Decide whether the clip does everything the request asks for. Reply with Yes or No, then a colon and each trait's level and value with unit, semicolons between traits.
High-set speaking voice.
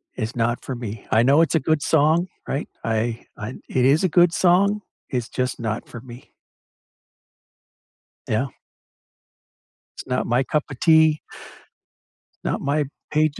No: low, 135 Hz